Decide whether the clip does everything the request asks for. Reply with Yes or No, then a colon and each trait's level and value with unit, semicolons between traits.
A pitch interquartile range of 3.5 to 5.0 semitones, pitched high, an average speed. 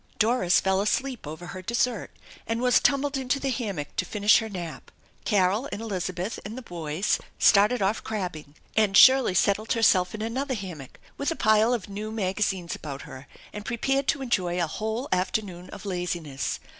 Yes: average, 4.6 semitones; high, 205 Hz; average, 180 wpm